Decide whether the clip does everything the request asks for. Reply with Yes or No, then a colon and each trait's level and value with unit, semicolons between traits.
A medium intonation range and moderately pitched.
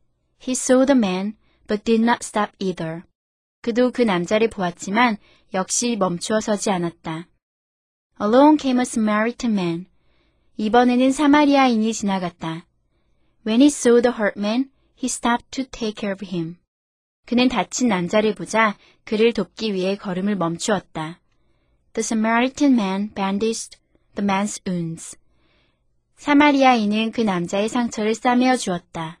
No: average, 4.6 semitones; high, 215 Hz